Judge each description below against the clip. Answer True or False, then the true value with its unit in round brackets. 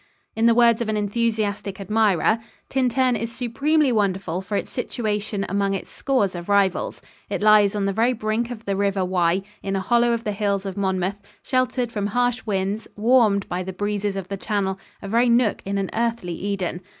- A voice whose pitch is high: True (205 Hz)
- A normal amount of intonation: True (3.1 semitones)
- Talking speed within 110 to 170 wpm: False (195 wpm)